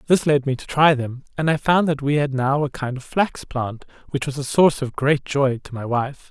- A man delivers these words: Yes, male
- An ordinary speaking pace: No, fast, 265 wpm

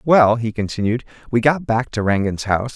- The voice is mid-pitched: No, low, 115 Hz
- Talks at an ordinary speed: Yes, average, 195 wpm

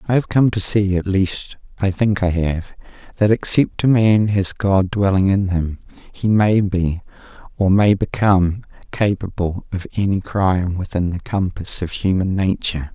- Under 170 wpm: Yes, average, 160 wpm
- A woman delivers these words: No, male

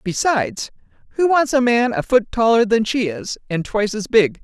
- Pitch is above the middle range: Yes, high, 230 Hz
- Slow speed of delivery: No, fast, 205 wpm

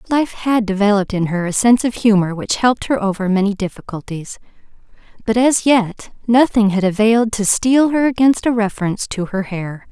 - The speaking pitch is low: No, high, 215 Hz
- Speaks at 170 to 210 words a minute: Yes, average, 180 wpm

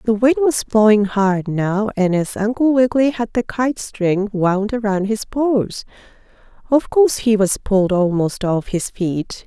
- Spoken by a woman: Yes, female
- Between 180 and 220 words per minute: No, average, 170 wpm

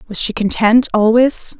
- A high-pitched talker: Yes, high, 225 Hz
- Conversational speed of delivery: Yes, average, 150 wpm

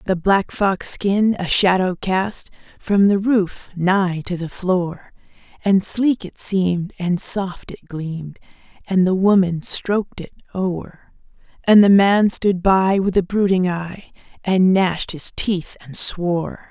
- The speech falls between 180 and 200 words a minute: No, average, 155 wpm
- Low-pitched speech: No, medium, 185 Hz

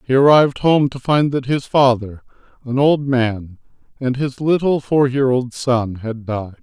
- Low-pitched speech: Yes, low, 130 Hz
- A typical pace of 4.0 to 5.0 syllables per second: Yes, 4.3 syllables/s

